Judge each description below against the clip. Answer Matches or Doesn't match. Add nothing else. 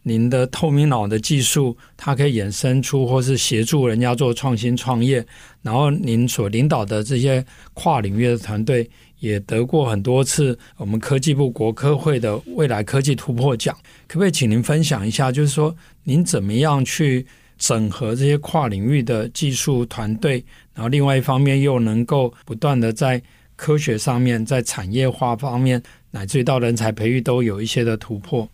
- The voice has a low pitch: Matches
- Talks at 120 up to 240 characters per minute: Doesn't match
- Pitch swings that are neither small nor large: Matches